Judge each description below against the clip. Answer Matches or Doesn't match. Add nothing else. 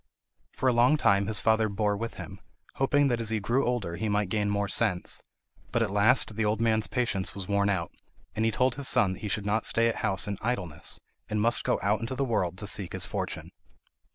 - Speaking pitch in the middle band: Doesn't match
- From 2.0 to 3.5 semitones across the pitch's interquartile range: Matches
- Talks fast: Matches